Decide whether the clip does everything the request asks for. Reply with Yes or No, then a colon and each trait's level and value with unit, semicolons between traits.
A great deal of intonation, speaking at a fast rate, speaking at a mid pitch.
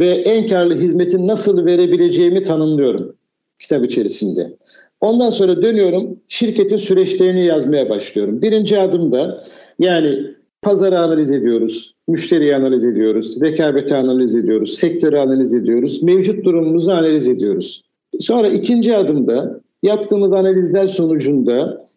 No: wide, 6.0 semitones; average, 110 wpm; medium, 175 Hz